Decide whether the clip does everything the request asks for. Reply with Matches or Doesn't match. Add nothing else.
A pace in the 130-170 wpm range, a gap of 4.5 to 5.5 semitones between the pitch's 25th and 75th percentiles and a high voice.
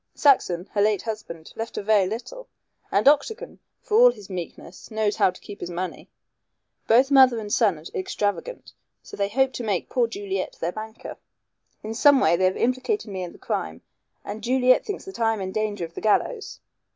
Doesn't match